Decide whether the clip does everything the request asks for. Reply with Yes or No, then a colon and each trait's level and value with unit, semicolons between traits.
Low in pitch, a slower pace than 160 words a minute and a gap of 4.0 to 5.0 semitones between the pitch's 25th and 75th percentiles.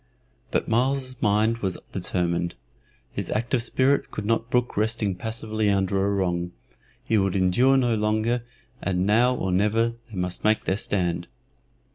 No: low, 105 Hz; average, 150 wpm; average, 3.5 semitones